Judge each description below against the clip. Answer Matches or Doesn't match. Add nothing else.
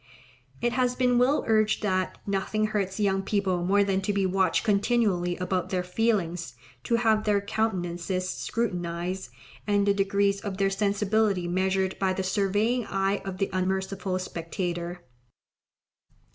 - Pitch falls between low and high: Doesn't match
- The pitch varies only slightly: Matches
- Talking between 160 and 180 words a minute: Doesn't match